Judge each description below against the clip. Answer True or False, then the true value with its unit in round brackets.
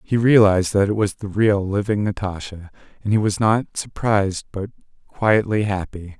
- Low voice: True (100 Hz)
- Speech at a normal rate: True (165 wpm)